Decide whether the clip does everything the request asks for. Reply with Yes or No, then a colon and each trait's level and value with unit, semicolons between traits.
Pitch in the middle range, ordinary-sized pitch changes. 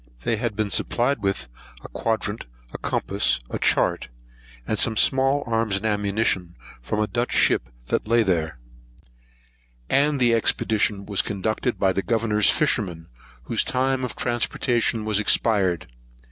No: low, 110 Hz; average, 3.3 semitones